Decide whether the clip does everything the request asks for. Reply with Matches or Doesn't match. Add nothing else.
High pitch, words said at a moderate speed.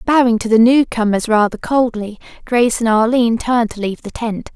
Matches